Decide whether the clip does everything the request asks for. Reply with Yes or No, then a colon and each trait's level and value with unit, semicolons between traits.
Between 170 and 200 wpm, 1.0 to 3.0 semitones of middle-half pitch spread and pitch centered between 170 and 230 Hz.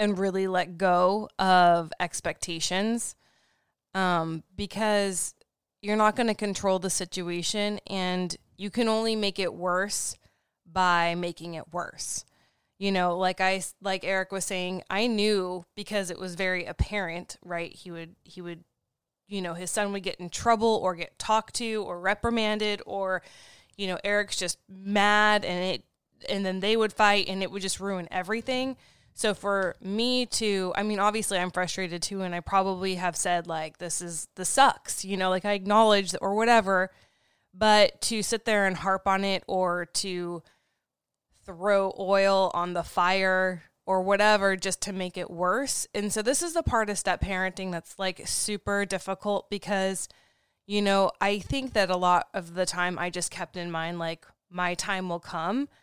Yes: average, 175 wpm; narrow, 2.4 semitones; high, 190 Hz